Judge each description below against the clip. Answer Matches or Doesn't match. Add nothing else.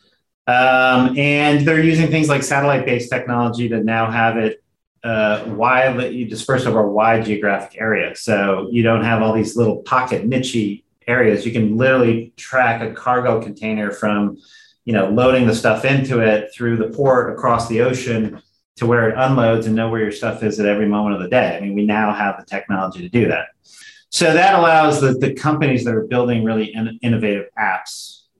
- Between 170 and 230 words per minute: Matches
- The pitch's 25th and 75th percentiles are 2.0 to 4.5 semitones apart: Matches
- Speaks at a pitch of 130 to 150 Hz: Doesn't match